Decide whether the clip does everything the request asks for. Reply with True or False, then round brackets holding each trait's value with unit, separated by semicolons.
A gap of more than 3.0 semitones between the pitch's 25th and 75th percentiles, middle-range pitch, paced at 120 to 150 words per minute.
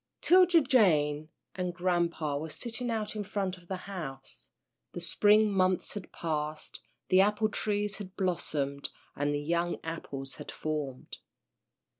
True (5.2 semitones; 180 Hz; 140 wpm)